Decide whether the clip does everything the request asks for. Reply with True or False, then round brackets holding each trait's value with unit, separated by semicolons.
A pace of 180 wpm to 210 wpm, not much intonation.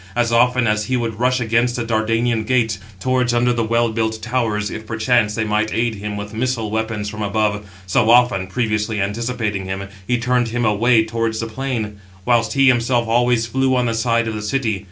True (200 wpm; 2.1 semitones)